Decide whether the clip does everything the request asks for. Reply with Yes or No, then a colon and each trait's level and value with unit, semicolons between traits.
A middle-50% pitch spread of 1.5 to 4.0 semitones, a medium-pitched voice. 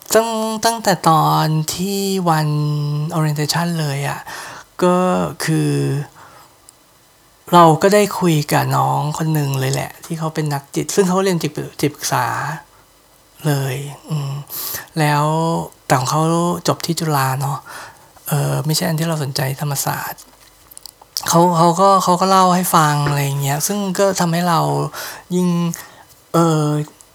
Yes: average, 3.3 semitones; medium, 155 Hz